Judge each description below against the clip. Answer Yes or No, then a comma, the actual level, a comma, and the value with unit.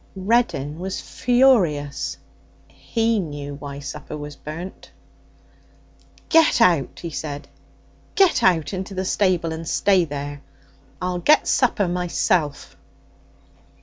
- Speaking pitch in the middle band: Yes, medium, 175 Hz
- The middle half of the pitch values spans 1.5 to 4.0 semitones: No, average, 5.0 semitones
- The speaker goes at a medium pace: No, slow, 110 wpm